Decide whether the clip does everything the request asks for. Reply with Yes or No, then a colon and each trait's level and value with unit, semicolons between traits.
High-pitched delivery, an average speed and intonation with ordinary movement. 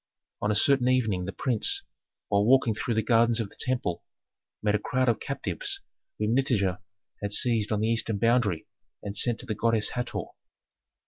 No: low, 115 Hz; average, 180 wpm; average, 3.1 semitones